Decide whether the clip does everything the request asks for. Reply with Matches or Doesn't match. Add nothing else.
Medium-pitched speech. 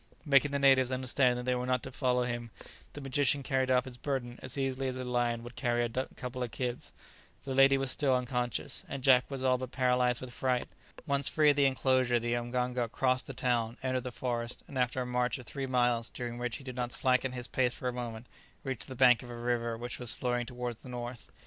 Doesn't match